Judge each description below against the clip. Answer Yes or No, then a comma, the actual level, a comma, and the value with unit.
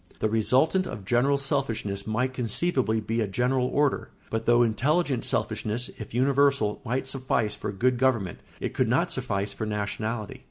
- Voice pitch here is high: No, low, 120 Hz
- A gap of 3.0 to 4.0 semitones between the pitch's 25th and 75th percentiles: Yes, average, 3.6 semitones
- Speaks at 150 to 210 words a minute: Yes, average, 160 wpm